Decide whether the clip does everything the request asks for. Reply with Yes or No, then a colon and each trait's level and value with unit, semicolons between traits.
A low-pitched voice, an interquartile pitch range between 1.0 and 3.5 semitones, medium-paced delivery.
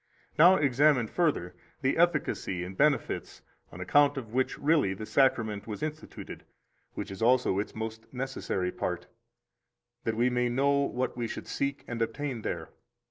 No: low, 125 Hz; average, 4.3 semitones; average, 155 wpm